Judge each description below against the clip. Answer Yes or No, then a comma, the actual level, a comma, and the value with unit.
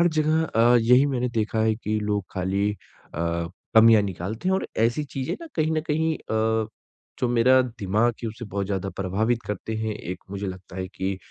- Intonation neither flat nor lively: Yes, average, 3.8 semitones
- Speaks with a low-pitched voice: Yes, low, 110 Hz